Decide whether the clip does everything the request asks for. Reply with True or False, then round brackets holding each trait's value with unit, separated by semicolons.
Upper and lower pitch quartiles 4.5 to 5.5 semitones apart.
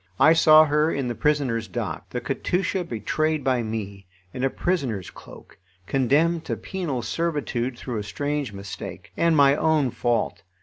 True (4.9 semitones)